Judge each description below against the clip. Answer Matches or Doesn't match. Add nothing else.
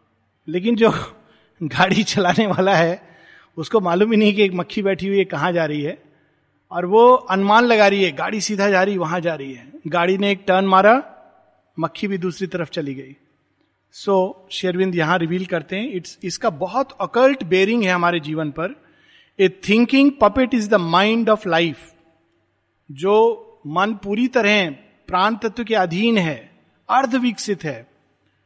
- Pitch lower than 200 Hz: Matches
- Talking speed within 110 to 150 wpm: Doesn't match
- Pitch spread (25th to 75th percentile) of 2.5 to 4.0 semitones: Doesn't match